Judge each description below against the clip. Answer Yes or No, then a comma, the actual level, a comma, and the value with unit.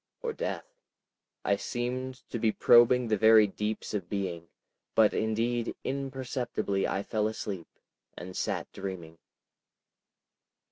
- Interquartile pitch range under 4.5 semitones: Yes, average, 3.6 semitones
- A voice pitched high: No, low, 110 Hz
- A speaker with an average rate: No, slow, 120 wpm